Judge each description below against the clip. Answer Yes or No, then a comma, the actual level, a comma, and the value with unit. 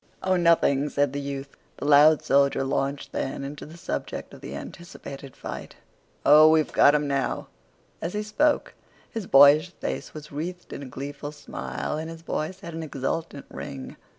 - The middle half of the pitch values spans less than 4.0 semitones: Yes, average, 2.8 semitones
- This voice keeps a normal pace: Yes, average, 175 wpm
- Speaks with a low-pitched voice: No, medium, 150 Hz